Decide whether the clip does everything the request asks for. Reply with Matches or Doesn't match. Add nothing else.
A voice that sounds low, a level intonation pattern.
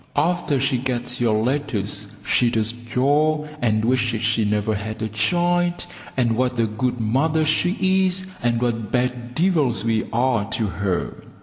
Doesn't match